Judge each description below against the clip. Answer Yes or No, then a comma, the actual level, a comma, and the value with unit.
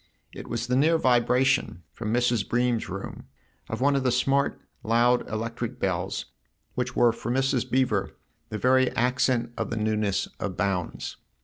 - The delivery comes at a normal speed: Yes, average, 155 wpm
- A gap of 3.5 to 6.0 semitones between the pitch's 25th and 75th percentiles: No, average, 2.8 semitones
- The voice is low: Yes, low, 120 Hz